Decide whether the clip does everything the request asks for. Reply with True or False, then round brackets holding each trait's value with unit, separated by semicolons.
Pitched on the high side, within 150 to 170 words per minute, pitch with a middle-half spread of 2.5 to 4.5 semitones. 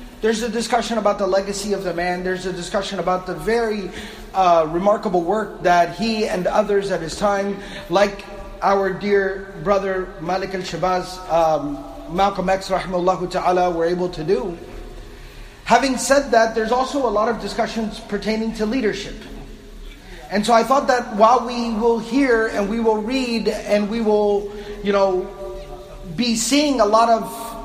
True (200 Hz; 165 wpm; 3.4 semitones)